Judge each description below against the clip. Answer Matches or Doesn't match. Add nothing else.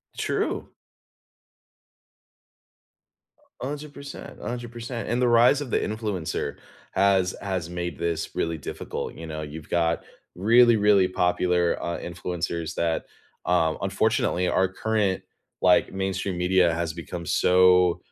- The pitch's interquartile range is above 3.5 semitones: Matches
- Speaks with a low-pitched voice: Matches